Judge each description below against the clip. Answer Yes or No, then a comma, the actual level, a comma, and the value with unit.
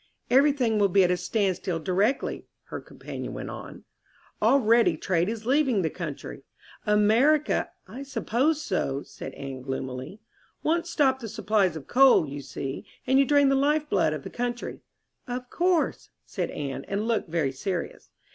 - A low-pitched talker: No, high, 215 Hz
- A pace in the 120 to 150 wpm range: No, average, 165 wpm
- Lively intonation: Yes, wide, 8.3 semitones